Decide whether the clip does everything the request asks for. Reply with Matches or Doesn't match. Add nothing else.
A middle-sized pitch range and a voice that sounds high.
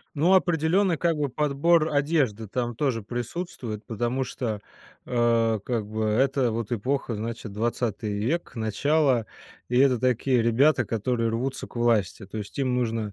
Doesn't match